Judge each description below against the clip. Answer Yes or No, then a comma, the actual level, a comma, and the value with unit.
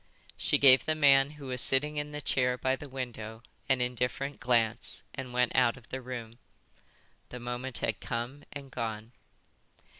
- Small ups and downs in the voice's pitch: Yes, narrow, 2.1 semitones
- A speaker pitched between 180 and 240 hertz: No, low, 125 Hz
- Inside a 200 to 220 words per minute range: No, average, 170 wpm